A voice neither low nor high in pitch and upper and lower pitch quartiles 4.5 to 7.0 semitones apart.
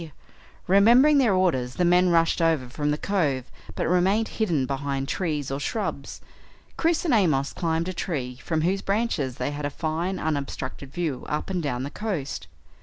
Yes: medium, 165 Hz; average, 5.2 semitones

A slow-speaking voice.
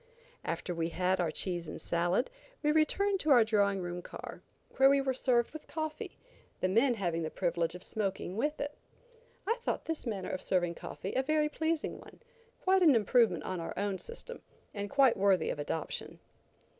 No: average, 185 wpm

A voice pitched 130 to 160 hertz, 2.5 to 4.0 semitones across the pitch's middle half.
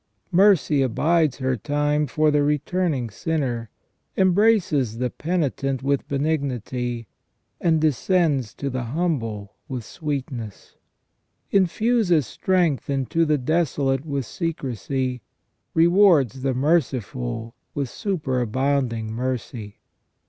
No: medium, 140 Hz; average, 4.5 semitones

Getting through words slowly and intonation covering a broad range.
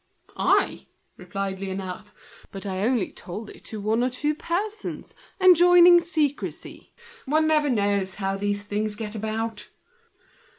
Yes: slow, 130 wpm; wide, 7.3 semitones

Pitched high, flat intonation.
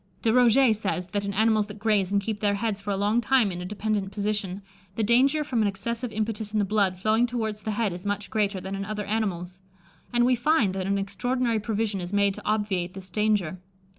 Yes: high, 210 Hz; narrow, 2.1 semitones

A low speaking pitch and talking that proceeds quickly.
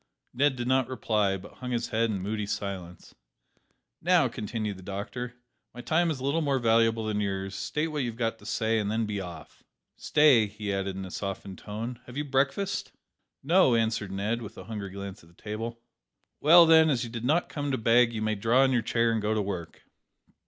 Yes: low, 115 Hz; fast, 215 wpm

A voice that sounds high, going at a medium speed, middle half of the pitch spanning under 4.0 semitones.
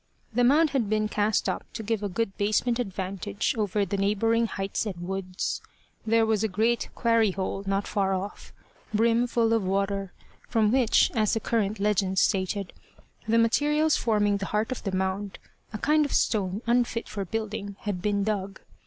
Yes: high, 210 Hz; average, 180 wpm; narrow, 2.6 semitones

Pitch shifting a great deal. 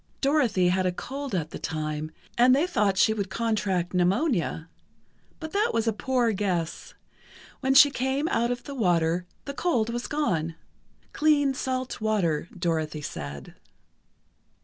Yes: wide, 7.2 semitones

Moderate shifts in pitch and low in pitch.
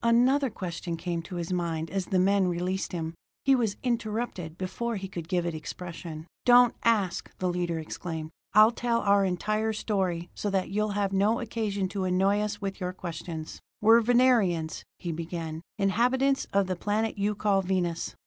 No: average, 3.7 semitones; high, 195 Hz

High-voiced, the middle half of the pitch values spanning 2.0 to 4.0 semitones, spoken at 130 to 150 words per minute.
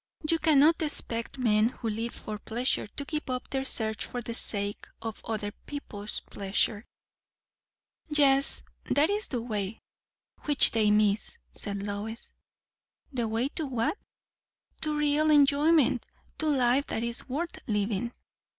No: high, 240 Hz; average, 5.1 semitones; average, 140 wpm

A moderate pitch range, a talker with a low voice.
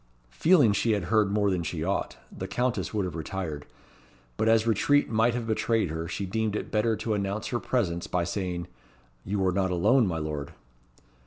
Yes: average, 4.1 semitones; low, 100 Hz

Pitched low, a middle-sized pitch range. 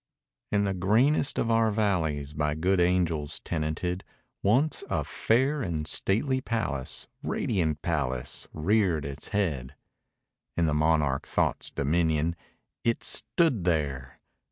No: very low, 85 Hz; wide, 5.9 semitones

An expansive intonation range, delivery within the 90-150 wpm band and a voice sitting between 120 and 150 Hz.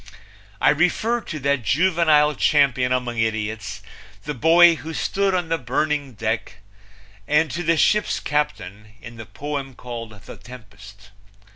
Yes: wide, 6.2 semitones; average, 140 wpm; medium, 140 Hz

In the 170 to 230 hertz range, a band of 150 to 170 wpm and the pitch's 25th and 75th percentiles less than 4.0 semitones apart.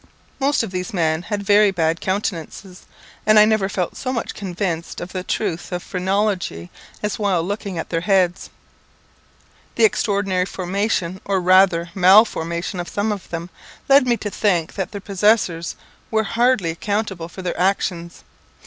Yes: high, 190 Hz; average, 160 wpm; average, 3.0 semitones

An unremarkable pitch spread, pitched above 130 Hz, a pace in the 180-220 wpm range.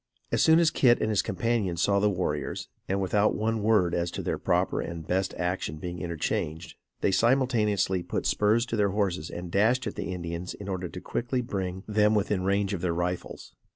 No: average, 3.5 semitones; very low, 95 Hz; average, 200 wpm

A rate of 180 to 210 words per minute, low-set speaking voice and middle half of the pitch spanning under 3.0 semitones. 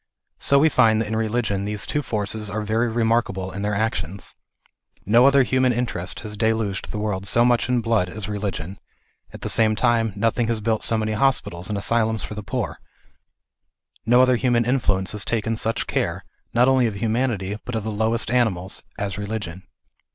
Yes: average, 190 wpm; low, 110 Hz; narrow, 2.5 semitones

